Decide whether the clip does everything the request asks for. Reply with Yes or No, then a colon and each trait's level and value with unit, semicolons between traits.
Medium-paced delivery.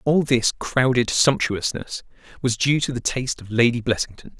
Yes: average, 165 wpm